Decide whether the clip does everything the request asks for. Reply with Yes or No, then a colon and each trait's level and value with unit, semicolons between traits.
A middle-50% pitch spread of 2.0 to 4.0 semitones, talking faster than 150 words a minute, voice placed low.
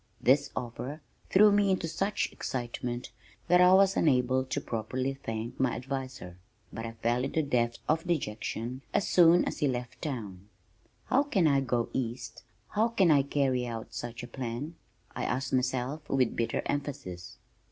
No: average, 4.4 semitones; average, 165 wpm; low, 130 Hz